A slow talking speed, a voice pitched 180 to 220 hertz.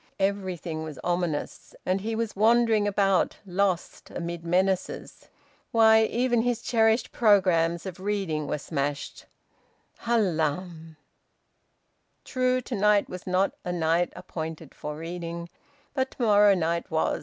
Yes: slow, 120 wpm; medium, 185 Hz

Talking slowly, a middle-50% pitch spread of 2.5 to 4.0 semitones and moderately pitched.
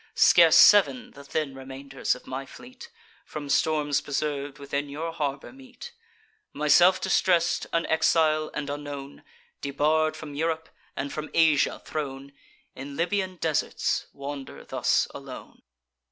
Yes: slow, 125 wpm; average, 2.8 semitones; medium, 150 Hz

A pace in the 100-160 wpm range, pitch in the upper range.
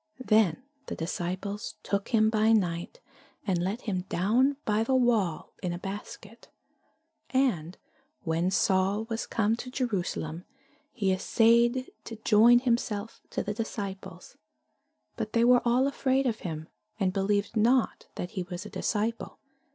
Yes: average, 145 wpm; high, 210 Hz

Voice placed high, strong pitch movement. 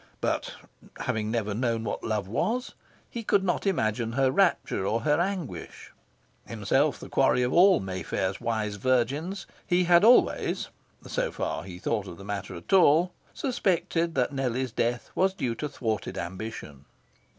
No: low, 125 Hz; wide, 8.4 semitones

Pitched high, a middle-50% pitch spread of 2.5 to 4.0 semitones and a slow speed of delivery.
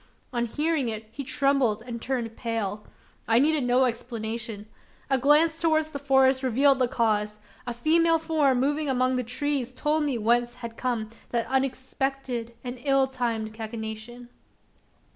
No: very high, 250 Hz; average, 3.1 semitones; average, 150 wpm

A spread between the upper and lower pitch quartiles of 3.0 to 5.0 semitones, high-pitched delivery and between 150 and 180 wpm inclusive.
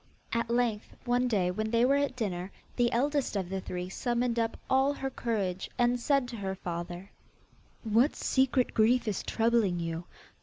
Yes: average, 4.5 semitones; high, 230 Hz; average, 175 wpm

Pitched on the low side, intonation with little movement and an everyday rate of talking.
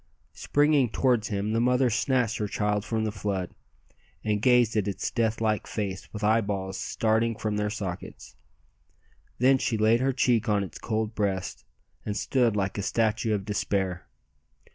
Yes: low, 110 Hz; narrow, 2.2 semitones; average, 165 wpm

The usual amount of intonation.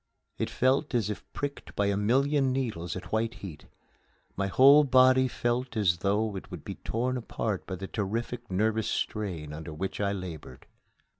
Yes: average, 5.0 semitones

